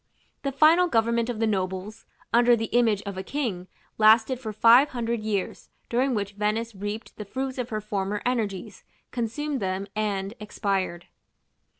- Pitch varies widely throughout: No, average, 3.2 semitones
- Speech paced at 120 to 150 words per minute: No, average, 160 wpm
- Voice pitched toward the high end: Yes, high, 220 Hz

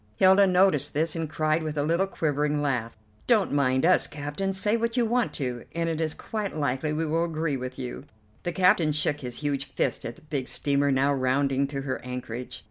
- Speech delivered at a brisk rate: Yes, fast, 210 wpm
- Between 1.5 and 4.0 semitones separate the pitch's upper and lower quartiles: Yes, average, 3.7 semitones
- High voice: No, medium, 150 Hz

